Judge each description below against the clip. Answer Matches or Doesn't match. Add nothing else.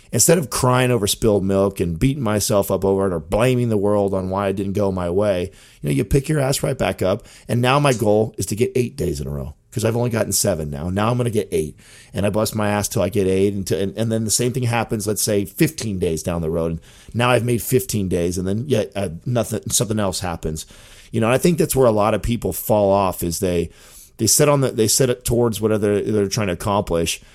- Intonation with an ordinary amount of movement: Matches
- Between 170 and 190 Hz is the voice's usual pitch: Doesn't match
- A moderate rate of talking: Doesn't match